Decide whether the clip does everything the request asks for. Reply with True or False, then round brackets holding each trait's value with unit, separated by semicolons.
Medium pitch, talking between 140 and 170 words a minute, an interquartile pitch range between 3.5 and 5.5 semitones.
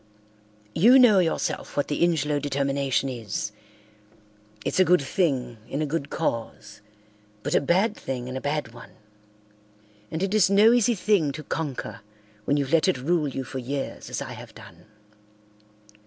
True (145 Hz; 165 wpm; 5.1 semitones)